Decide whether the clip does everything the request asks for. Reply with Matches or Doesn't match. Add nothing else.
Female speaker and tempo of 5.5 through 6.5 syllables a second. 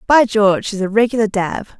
Matches